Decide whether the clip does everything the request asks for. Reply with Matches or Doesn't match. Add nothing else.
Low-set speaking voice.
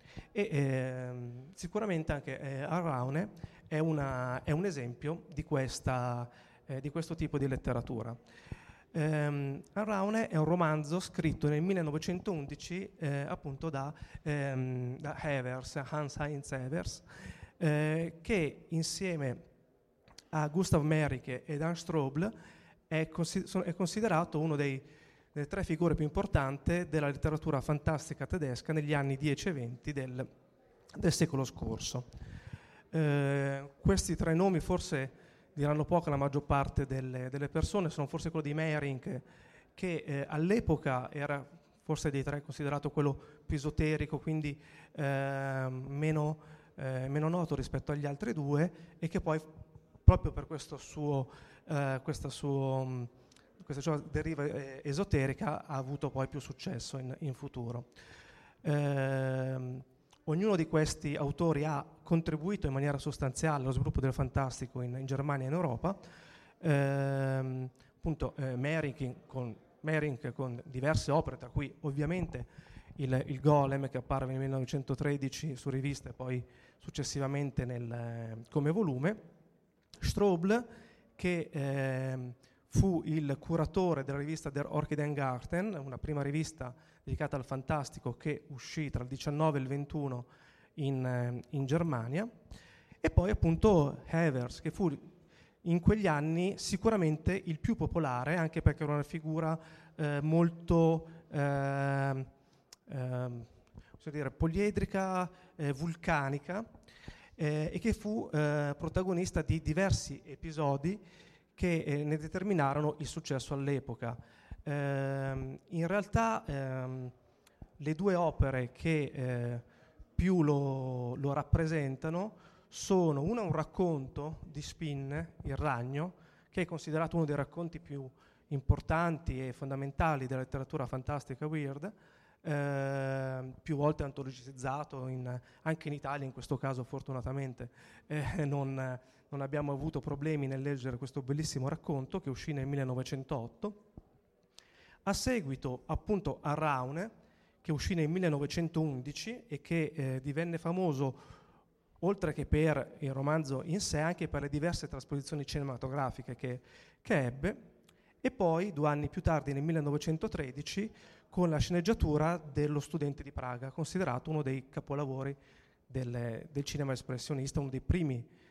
Doesn't match